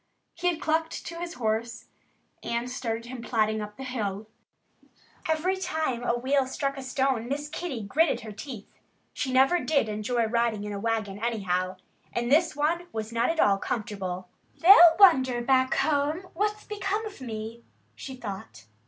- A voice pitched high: Yes, very high, 250 Hz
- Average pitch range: No, wide, 6.0 semitones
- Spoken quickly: No, average, 165 wpm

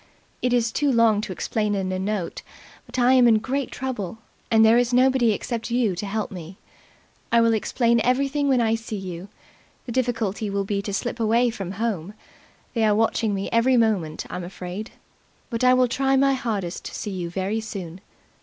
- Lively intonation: No, average, 3.7 semitones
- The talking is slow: No, average, 190 wpm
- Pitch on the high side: Yes, high, 225 Hz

